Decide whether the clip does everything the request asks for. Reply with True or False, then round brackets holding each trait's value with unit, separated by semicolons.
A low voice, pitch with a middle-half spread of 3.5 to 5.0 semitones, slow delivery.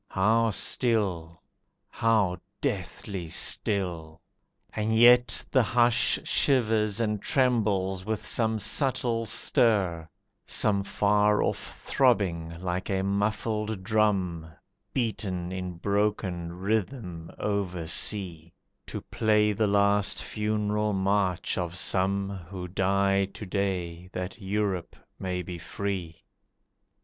False (100 Hz; 2.9 semitones; 100 wpm)